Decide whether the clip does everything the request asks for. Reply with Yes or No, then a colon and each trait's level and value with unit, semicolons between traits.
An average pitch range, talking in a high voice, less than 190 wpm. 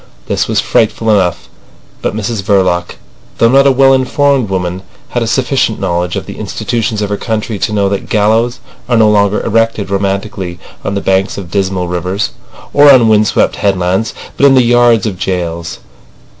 No: average, 3.4 semitones; low, 105 Hz; average, 180 wpm